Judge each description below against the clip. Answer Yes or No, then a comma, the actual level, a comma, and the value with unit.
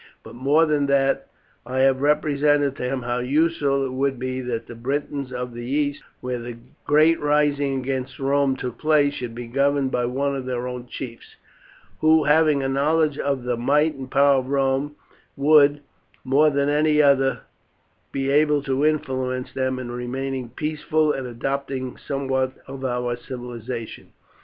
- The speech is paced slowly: No, average, 165 wpm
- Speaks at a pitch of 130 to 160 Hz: Yes, low, 135 Hz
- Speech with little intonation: Yes, narrow, 2.3 semitones